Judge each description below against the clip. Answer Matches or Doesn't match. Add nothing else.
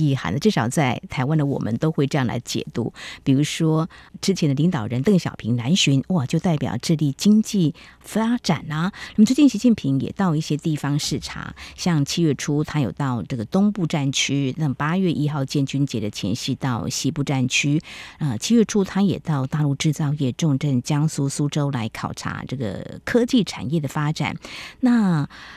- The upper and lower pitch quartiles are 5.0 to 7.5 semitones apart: Doesn't match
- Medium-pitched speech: Matches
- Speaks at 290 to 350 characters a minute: Doesn't match